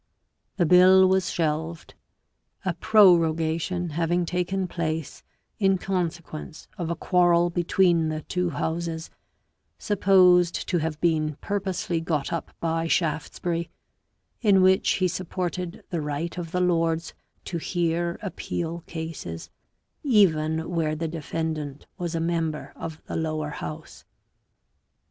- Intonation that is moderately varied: No, narrow, 1.9 semitones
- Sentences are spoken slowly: Yes, slow, 125 wpm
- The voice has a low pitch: No, medium, 170 Hz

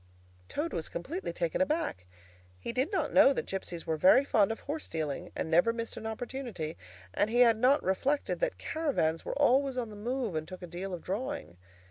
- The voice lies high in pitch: Yes, high, 230 Hz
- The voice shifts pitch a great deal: Yes, wide, 7.9 semitones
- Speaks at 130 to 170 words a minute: No, average, 200 wpm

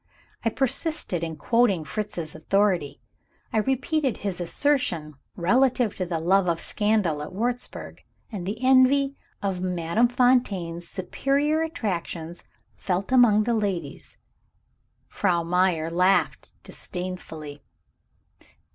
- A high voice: Yes, high, 195 Hz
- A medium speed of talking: No, slow, 110 wpm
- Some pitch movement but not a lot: No, wide, 6.3 semitones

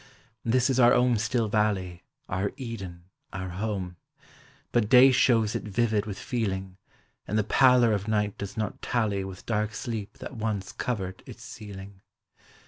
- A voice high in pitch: No, low, 105 Hz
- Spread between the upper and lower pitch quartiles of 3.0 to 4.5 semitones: Yes, average, 3.4 semitones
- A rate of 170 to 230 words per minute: No, average, 155 wpm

